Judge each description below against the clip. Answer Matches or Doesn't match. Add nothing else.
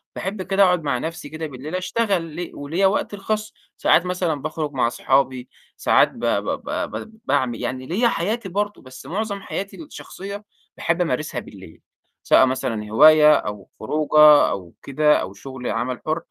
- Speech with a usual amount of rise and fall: Doesn't match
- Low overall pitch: Doesn't match